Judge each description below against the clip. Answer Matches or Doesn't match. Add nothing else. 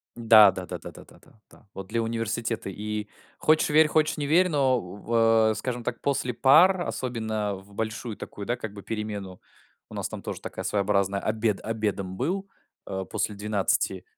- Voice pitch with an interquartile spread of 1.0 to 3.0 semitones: Doesn't match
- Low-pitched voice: Matches